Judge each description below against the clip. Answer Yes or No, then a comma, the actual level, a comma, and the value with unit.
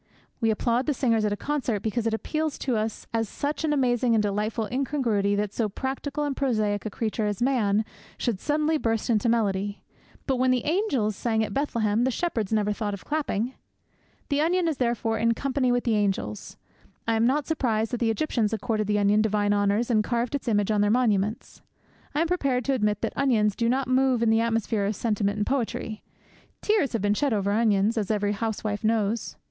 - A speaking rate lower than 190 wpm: No, fast, 205 wpm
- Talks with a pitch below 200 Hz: No, high, 225 Hz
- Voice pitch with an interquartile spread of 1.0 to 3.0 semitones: No, average, 3.7 semitones